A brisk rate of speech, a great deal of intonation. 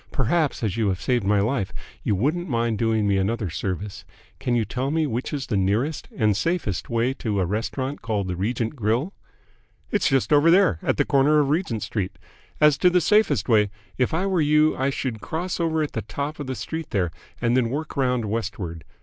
Yes: fast, 210 wpm; wide, 6.1 semitones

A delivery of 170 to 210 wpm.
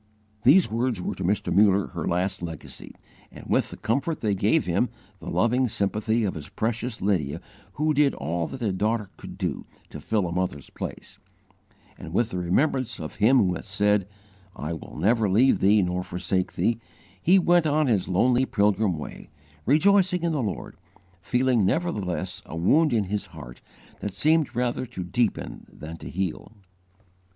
Yes: average, 175 wpm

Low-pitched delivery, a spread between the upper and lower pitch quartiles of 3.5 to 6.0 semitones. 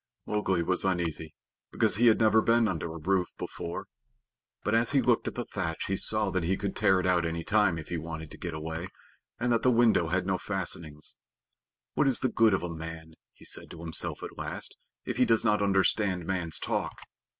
Yes: very low, 95 Hz; average, 4.5 semitones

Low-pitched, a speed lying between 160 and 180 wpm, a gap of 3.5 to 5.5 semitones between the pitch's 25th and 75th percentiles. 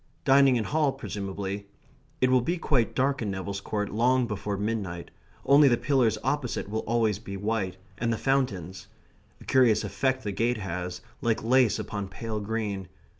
Yes: low, 110 Hz; average, 170 wpm; average, 4.4 semitones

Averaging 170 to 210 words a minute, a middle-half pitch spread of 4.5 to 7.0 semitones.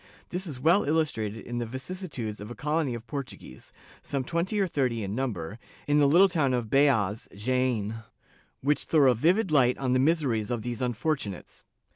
Yes: average, 180 wpm; average, 5.3 semitones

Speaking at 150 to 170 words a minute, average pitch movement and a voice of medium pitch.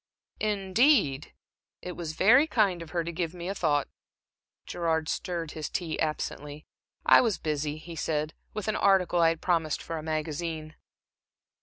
Yes: average, 160 wpm; average, 3.0 semitones; medium, 165 Hz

